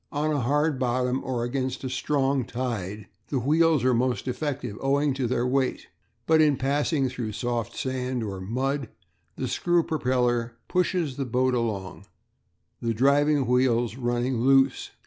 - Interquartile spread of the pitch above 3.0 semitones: No, average, 2.7 semitones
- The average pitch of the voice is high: No, low, 130 Hz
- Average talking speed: Yes, average, 150 wpm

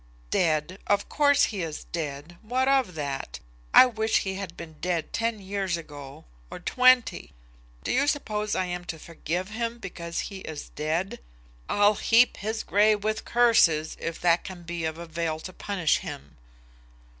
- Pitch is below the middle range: No, medium, 185 Hz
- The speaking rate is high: No, average, 165 wpm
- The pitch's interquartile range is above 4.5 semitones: Yes, average, 4.9 semitones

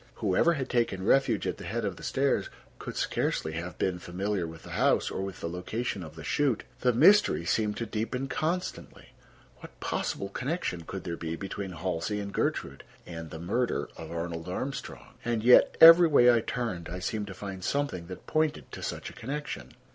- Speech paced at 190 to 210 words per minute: Yes, average, 195 wpm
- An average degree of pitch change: No, wide, 6.2 semitones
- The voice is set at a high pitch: No, low, 100 Hz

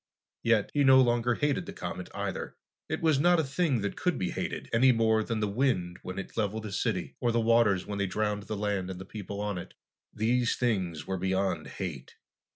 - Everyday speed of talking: No, fast, 215 wpm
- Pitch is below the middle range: Yes, low, 110 Hz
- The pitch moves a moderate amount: Yes, average, 3.8 semitones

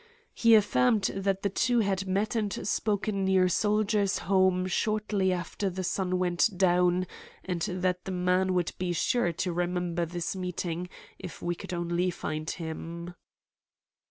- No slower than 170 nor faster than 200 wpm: No, average, 150 wpm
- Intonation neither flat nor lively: No, narrow, 2.0 semitones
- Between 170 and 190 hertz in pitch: Yes, medium, 185 Hz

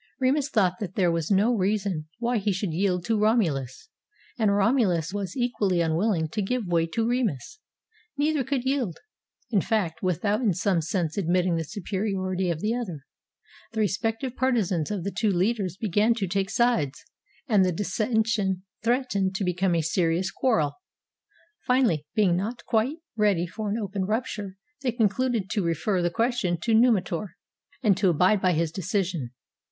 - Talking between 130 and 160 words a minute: No, average, 170 wpm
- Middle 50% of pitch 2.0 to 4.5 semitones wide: Yes, average, 4.2 semitones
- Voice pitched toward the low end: No, high, 200 Hz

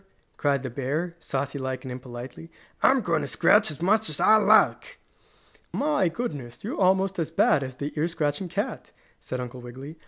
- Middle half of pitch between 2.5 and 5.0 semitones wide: No, wide, 5.5 semitones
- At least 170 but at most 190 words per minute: Yes, average, 180 wpm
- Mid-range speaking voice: Yes, medium, 145 Hz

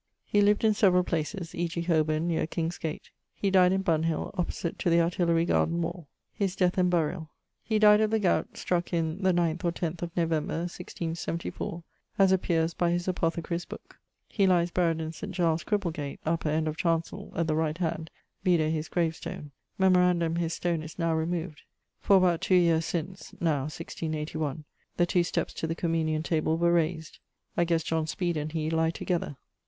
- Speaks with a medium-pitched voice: Yes, medium, 170 Hz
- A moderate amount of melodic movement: No, narrow, 1.8 semitones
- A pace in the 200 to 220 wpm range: No, average, 190 wpm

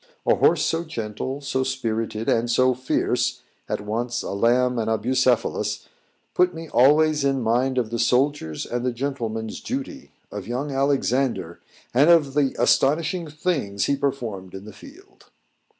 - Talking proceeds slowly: No, average, 155 wpm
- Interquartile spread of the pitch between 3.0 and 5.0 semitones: Yes, average, 4.2 semitones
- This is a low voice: Yes, low, 130 Hz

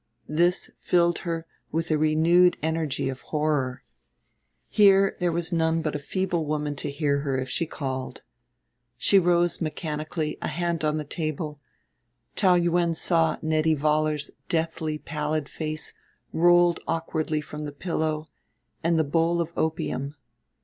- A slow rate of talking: No, average, 145 wpm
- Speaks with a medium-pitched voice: Yes, medium, 160 Hz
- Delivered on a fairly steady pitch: Yes, narrow, 2.1 semitones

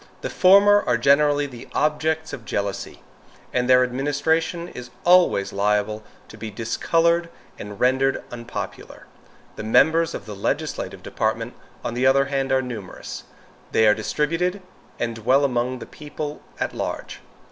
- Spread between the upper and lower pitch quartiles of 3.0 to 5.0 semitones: No, wide, 5.4 semitones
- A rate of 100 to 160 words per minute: Yes, average, 145 wpm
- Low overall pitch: Yes, low, 130 Hz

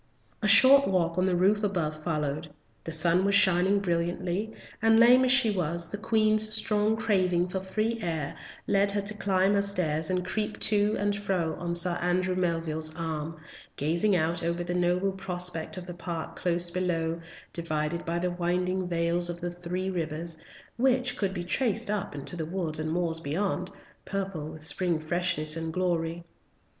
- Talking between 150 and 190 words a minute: Yes, average, 175 wpm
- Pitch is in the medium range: Yes, medium, 180 Hz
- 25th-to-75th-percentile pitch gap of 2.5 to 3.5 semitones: Yes, average, 3.0 semitones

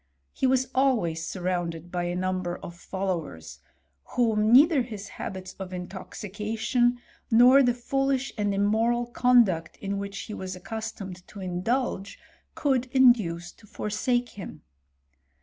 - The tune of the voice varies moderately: Yes, average, 4.8 semitones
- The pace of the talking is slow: Yes, slow, 130 wpm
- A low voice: No, high, 210 Hz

